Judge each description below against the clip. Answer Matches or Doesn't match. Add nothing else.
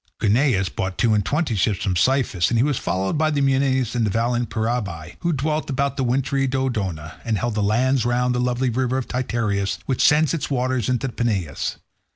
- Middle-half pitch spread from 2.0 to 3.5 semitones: Doesn't match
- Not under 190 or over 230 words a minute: Matches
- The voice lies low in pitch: Matches